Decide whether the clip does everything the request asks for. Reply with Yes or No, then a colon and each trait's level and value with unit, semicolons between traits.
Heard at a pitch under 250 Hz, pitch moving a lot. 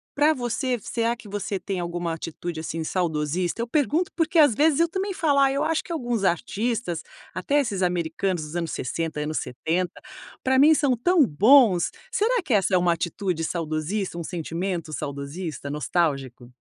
Yes: medium, 185 Hz; wide, 8.3 semitones